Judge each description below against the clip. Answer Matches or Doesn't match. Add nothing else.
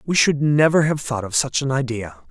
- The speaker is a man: Matches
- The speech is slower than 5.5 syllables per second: Matches